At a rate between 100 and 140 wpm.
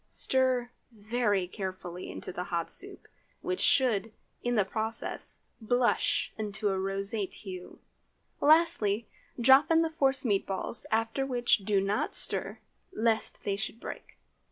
Yes: slow, 135 wpm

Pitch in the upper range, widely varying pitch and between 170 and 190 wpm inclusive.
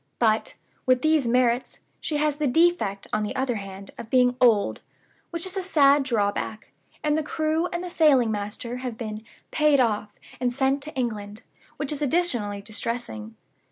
Yes: very high, 250 Hz; wide, 5.7 semitones; average, 175 wpm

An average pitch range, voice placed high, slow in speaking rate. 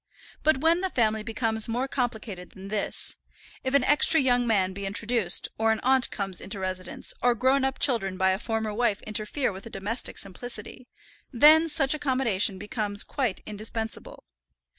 No: average, 4.4 semitones; high, 225 Hz; average, 165 wpm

